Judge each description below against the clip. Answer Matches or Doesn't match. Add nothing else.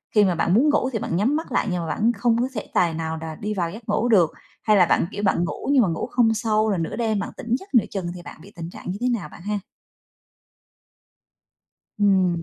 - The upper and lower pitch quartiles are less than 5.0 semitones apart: Matches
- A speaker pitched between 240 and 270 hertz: Doesn't match